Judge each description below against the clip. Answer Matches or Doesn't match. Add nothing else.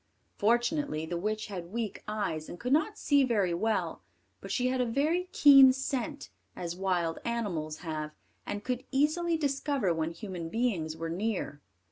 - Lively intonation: Matches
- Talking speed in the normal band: Matches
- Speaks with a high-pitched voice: Matches